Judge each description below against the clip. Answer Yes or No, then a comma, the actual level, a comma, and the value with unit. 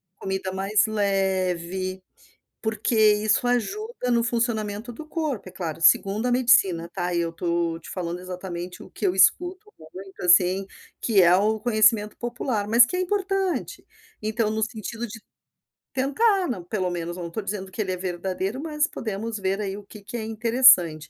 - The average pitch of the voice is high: Yes, high, 210 Hz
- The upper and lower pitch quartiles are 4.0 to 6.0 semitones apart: Yes, average, 4.4 semitones